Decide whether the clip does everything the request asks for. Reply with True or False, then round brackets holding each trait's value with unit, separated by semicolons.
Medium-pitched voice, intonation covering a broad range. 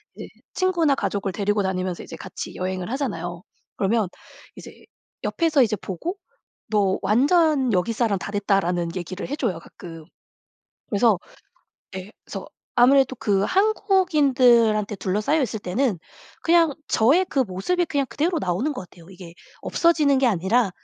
False (220 Hz; 7.1 semitones)